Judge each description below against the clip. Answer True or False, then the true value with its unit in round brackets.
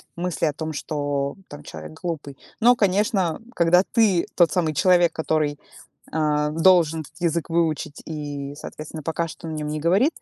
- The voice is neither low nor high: True (160 Hz)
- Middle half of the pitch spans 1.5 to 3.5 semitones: True (2.8 semitones)